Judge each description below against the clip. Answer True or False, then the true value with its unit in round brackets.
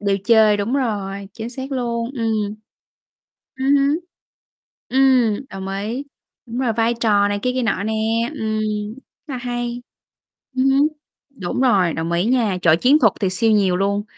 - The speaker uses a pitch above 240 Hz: False (225 Hz)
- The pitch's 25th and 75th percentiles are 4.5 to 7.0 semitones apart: False (3.9 semitones)